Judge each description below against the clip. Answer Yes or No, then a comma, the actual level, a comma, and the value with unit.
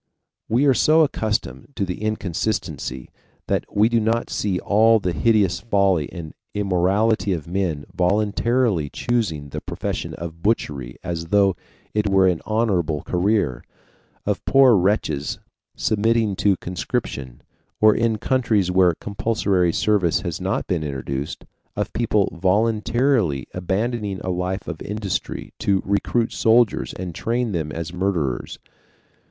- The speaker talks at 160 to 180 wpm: No, slow, 135 wpm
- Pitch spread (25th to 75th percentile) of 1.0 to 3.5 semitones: No, average, 4.2 semitones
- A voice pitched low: Yes, very low, 95 Hz